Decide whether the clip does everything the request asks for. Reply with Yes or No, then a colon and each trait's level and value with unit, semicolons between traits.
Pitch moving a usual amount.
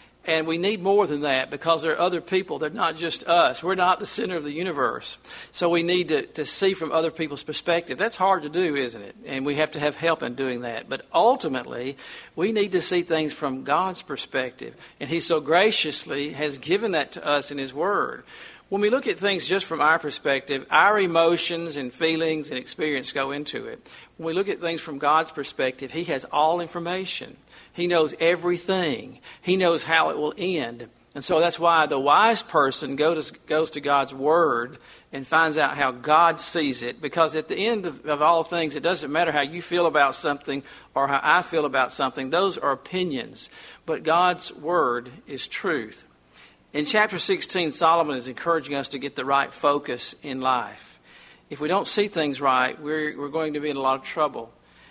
Yes: average, 3.5 semitones